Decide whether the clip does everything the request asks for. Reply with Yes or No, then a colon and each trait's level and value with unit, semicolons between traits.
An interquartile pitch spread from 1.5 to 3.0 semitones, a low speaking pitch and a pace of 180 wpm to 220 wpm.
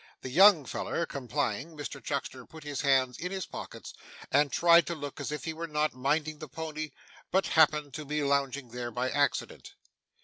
No: average, 2.7 semitones; medium, 150 Hz; average, 190 wpm